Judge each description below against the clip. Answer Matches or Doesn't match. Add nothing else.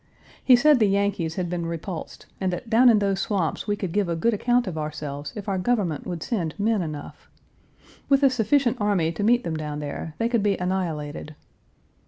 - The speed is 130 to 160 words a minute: Doesn't match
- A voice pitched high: Matches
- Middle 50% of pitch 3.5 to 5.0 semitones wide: Doesn't match